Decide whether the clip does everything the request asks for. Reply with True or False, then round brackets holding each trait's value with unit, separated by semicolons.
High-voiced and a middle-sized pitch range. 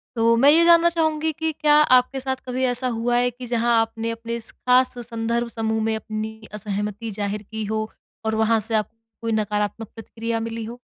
False (230 Hz; 2.2 semitones)